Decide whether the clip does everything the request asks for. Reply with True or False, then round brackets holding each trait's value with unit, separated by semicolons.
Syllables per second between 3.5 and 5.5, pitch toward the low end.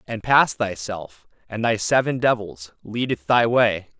True (4.0 syllables/s; 105 Hz)